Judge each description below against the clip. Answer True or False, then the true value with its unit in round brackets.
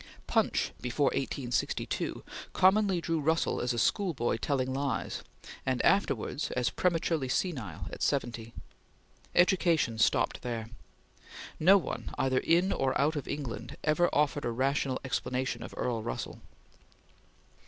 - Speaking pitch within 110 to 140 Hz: True (135 Hz)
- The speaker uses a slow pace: True (125 wpm)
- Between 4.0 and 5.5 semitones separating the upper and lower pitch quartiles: True (5.2 semitones)